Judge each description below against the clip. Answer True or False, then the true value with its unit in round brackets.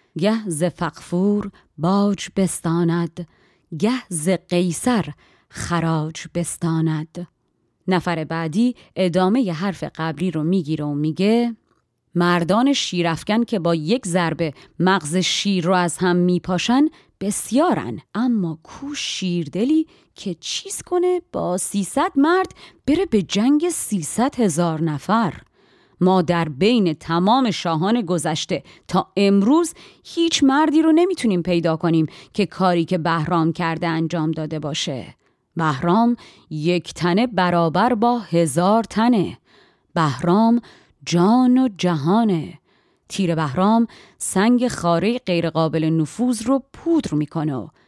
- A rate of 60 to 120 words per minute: True (115 wpm)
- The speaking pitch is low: False (180 Hz)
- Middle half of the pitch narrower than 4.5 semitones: False (5.4 semitones)